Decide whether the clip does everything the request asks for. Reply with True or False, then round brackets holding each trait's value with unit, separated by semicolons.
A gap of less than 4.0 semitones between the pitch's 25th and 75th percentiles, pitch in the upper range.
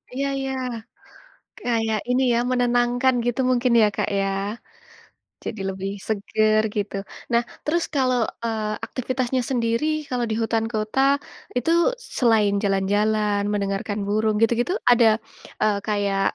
True (2.7 semitones; 225 Hz)